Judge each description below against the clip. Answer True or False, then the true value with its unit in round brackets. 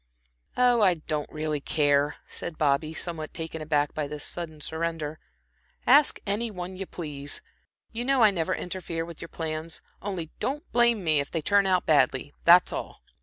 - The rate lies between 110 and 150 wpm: False (170 wpm)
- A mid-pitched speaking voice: True (165 Hz)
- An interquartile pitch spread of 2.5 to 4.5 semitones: True (3.8 semitones)